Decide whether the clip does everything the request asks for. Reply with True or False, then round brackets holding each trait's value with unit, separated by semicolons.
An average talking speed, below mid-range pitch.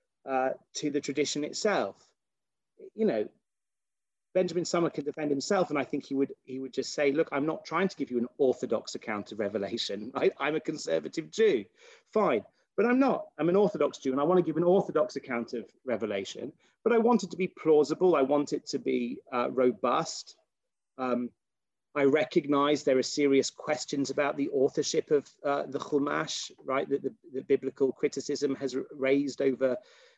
False (185 wpm; 145 Hz)